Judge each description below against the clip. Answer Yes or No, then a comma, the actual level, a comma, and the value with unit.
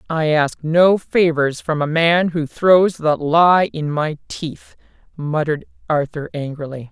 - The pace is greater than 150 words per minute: No, average, 145 wpm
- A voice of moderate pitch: Yes, medium, 155 Hz